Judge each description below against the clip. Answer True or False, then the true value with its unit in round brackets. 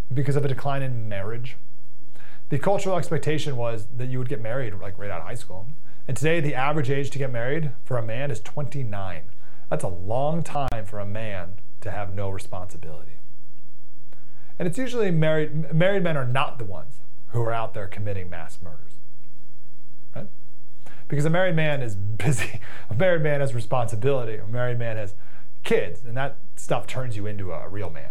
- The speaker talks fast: False (190 wpm)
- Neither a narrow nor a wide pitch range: False (5.7 semitones)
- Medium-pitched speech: False (125 Hz)